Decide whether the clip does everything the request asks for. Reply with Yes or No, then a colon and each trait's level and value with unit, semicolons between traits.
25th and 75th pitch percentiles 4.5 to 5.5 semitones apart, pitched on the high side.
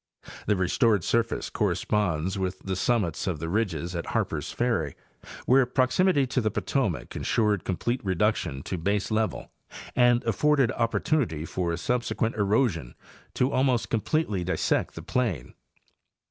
No: average, 5.2 semitones; low, 105 Hz